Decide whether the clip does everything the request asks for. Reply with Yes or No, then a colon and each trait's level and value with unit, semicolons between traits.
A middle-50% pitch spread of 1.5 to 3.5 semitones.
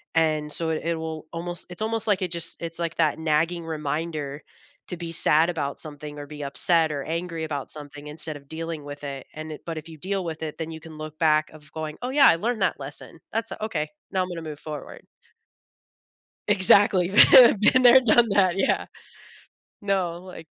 Yes: average, 2.9 semitones